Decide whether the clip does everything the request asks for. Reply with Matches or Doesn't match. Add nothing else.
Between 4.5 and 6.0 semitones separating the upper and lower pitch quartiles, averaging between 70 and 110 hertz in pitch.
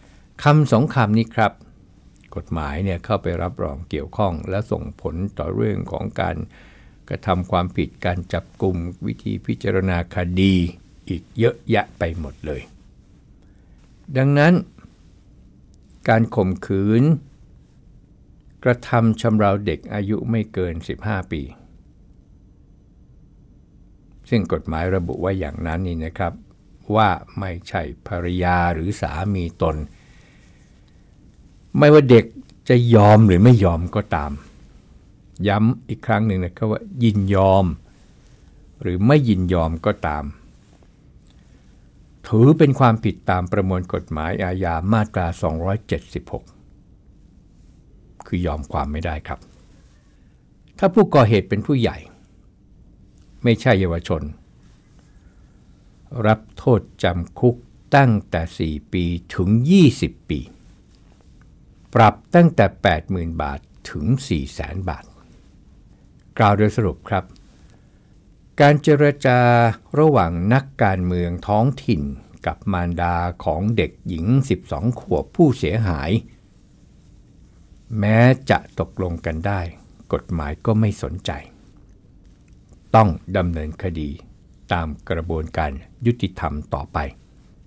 Matches